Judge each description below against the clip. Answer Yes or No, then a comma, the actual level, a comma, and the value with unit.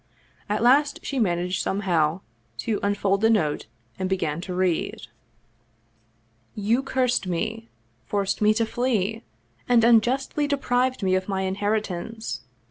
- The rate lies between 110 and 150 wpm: Yes, average, 140 wpm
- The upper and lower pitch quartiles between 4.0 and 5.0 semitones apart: Yes, average, 4.3 semitones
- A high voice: Yes, high, 205 Hz